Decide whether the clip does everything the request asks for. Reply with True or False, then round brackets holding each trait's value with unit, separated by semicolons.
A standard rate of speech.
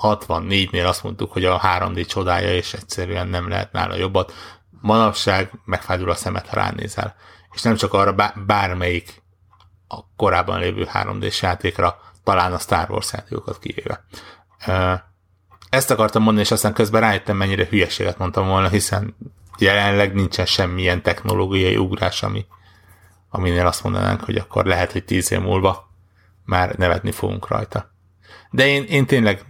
True (145 wpm)